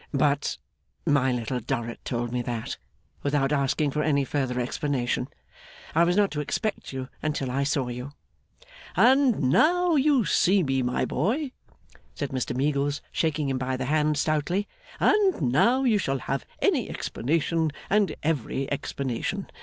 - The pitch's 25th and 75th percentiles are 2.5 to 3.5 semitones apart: No, average, 4.9 semitones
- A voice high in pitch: No, medium, 145 Hz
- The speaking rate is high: No, average, 155 wpm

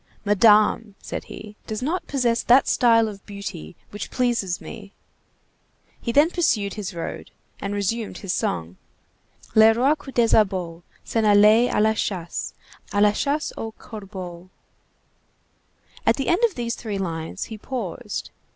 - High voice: Yes, high, 215 Hz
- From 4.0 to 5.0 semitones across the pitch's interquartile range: No, average, 3.2 semitones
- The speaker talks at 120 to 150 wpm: Yes, average, 140 wpm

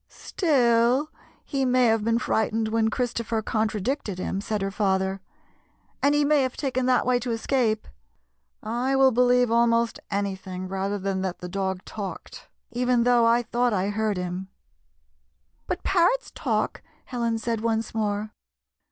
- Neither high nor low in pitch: No, high, 230 Hz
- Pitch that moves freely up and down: No, average, 3.5 semitones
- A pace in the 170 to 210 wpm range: No, average, 155 wpm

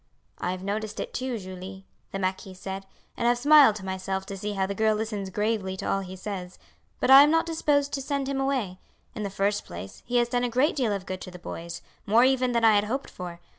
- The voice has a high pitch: Yes, high, 210 Hz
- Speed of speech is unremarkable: No, fast, 245 wpm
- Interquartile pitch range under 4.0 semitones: No, average, 4.6 semitones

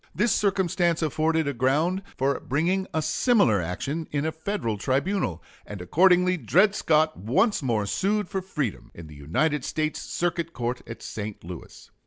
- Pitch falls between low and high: Yes, medium, 155 Hz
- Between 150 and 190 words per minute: Yes, average, 160 wpm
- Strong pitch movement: Yes, wide, 7.5 semitones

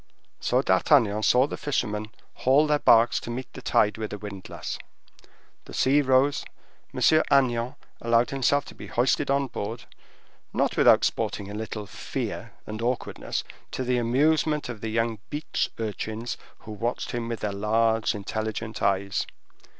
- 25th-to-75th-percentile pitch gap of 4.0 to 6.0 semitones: No, average, 3.3 semitones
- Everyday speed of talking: Yes, average, 155 wpm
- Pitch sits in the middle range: No, low, 115 Hz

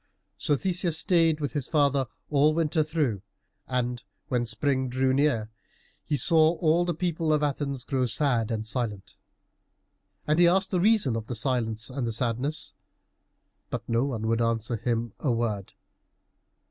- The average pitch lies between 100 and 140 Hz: Yes, low, 135 Hz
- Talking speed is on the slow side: No, average, 160 wpm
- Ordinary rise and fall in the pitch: Yes, average, 4.9 semitones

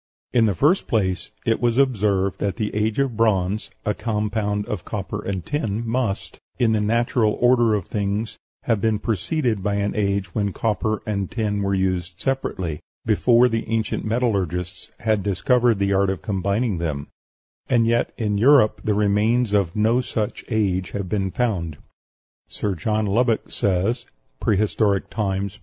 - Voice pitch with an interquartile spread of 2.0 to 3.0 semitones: Yes, average, 2.7 semitones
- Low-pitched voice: Yes, low, 105 Hz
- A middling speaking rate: Yes, average, 160 wpm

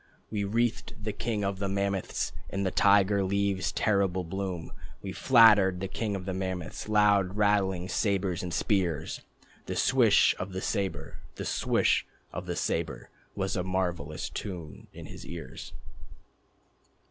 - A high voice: No, very low, 95 Hz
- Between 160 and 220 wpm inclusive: No, average, 145 wpm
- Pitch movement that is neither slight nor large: No, narrow, 1.7 semitones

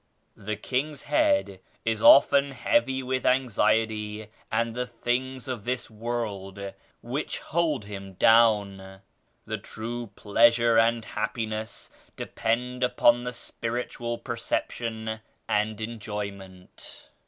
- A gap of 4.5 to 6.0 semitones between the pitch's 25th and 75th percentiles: No, narrow, 2.6 semitones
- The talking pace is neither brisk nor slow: No, slow, 110 wpm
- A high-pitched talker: No, low, 115 Hz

